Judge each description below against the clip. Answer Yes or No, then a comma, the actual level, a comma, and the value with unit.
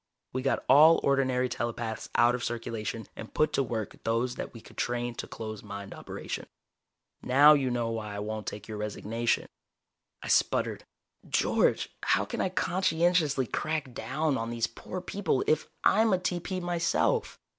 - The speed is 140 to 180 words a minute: Yes, average, 165 wpm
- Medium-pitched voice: No, low, 125 Hz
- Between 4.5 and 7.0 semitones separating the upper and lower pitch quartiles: Yes, wide, 5.6 semitones